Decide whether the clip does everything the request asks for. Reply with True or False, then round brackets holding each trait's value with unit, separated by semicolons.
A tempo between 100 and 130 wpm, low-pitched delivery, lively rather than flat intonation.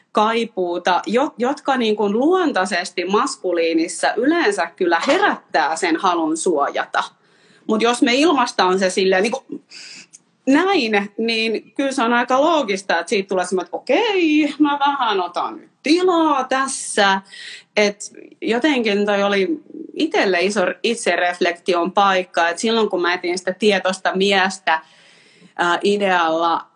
False (125 wpm; 210 Hz; 6.8 semitones)